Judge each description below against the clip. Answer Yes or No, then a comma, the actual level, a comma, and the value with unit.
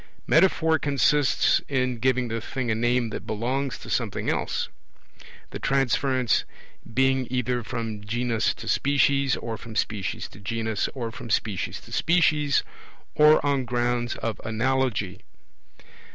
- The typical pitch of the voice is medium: No, low, 125 Hz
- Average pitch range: Yes, average, 3.1 semitones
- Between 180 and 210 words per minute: No, slow, 135 wpm